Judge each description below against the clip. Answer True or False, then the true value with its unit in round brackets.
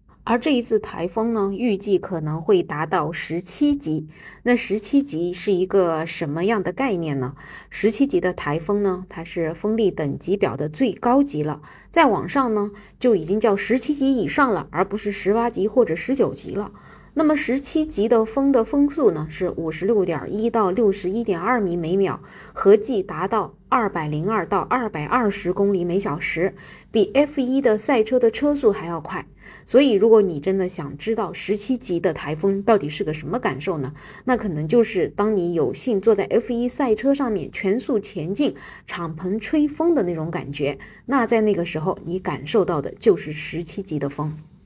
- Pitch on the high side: True (200 Hz)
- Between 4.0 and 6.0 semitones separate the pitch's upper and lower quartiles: True (5.5 semitones)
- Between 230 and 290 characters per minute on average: True (275 characters per minute)